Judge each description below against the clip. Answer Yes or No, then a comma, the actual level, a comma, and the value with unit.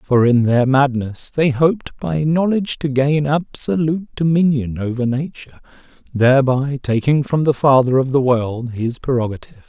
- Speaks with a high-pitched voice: No, low, 135 Hz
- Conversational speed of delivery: Yes, average, 150 wpm